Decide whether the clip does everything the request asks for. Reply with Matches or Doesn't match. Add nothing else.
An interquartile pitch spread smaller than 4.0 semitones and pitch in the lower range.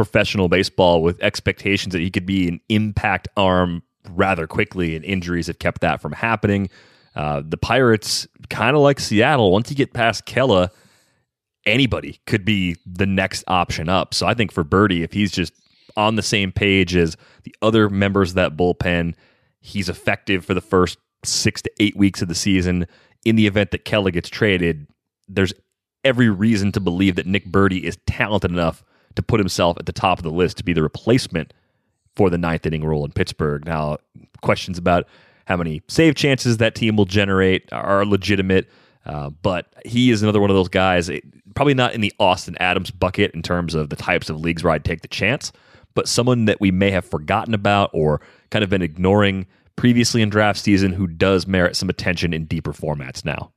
Matches